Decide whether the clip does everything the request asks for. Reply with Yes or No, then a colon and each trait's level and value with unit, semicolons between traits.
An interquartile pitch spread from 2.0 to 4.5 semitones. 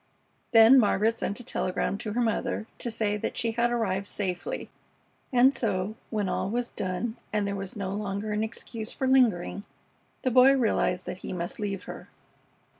Yes: average, 3.3 semitones